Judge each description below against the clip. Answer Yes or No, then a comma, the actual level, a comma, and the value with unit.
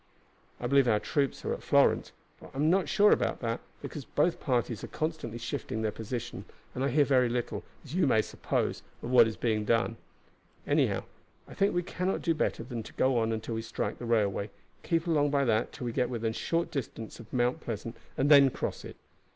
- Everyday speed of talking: No, fast, 215 wpm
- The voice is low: Yes, low, 125 Hz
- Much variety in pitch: No, average, 4.3 semitones